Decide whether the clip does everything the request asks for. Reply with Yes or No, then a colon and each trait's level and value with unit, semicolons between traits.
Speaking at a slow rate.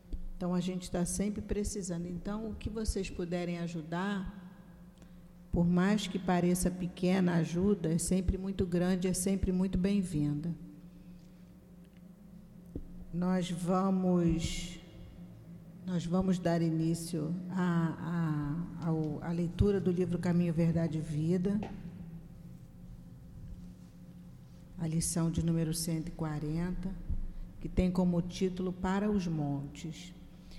Yes: slow, 110 wpm